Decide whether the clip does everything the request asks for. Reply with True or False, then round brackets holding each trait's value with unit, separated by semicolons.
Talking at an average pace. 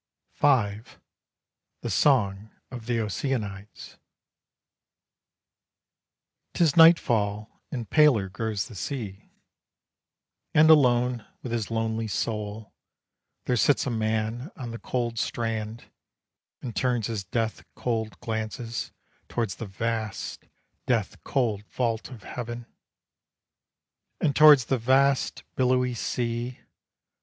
False (105 wpm)